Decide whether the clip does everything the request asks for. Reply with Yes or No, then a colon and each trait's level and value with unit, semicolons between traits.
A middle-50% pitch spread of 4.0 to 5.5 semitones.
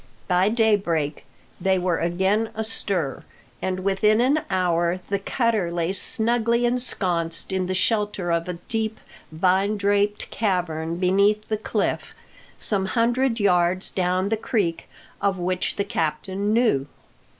No: average, 3.3 semitones